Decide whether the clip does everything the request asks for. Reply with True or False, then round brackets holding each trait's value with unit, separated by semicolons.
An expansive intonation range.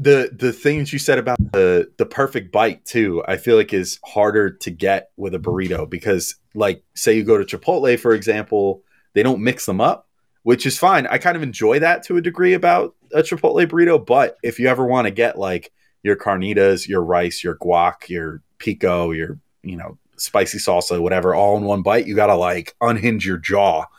True (7.9 semitones)